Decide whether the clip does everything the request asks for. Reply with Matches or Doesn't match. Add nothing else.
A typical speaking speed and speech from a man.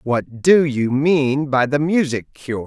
Matches